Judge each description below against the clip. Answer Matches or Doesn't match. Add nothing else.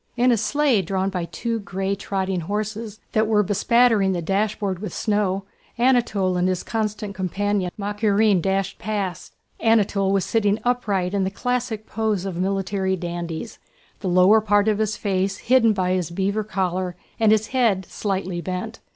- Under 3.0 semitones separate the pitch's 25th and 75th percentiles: Matches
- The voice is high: Matches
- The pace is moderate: Matches